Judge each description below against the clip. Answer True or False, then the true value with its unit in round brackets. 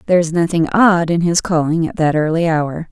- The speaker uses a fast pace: True (225 wpm)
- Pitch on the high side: False (165 Hz)